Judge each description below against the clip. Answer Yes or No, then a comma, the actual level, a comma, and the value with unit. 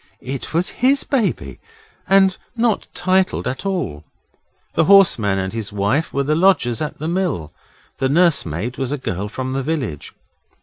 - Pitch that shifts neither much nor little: No, wide, 8.7 semitones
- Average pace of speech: Yes, average, 160 wpm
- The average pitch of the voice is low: No, medium, 145 Hz